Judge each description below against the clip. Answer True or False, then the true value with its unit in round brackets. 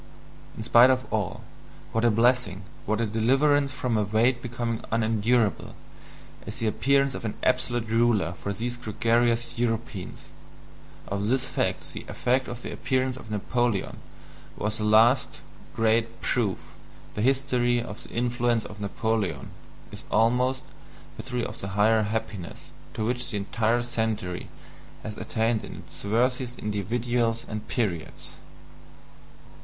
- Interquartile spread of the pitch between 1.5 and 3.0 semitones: True (2.4 semitones)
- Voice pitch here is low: True (115 Hz)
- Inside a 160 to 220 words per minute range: False (140 wpm)